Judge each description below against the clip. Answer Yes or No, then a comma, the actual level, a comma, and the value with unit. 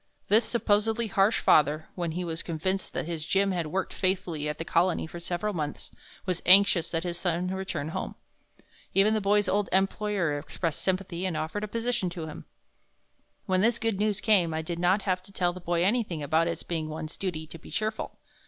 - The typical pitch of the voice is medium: Yes, medium, 180 Hz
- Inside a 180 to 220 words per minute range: Yes, average, 200 wpm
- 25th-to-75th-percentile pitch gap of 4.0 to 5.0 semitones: No, average, 3.4 semitones